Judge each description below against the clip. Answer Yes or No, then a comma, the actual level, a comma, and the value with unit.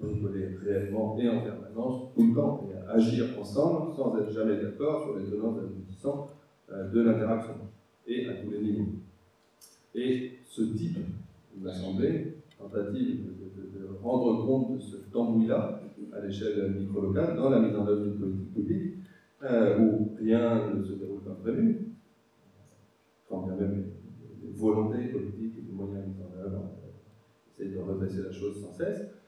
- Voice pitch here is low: Yes, low, 105 Hz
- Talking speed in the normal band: Yes, average, 160 wpm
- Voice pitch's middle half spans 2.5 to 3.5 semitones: Yes, average, 3.2 semitones